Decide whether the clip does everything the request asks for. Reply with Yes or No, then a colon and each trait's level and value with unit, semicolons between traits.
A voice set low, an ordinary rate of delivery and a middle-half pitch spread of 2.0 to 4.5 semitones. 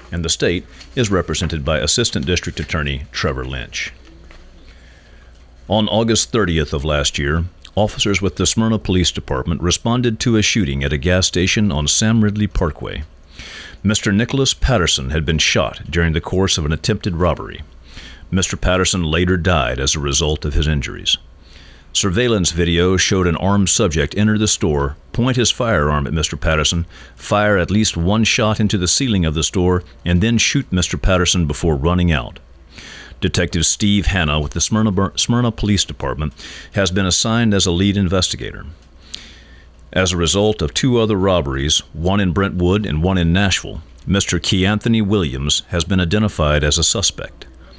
No: very low, 90 Hz; average, 165 wpm; average, 5.0 semitones